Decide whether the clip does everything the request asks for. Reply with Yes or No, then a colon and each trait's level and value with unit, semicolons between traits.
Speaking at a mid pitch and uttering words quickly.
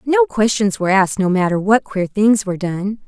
No: high, 200 Hz; fast, 215 wpm